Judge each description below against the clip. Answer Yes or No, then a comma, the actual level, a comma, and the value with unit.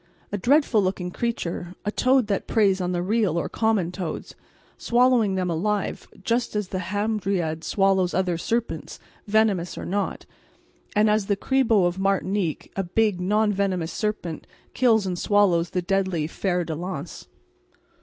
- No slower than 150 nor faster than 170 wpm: Yes, average, 155 wpm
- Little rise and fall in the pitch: No, average, 3.2 semitones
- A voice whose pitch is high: Yes, high, 195 Hz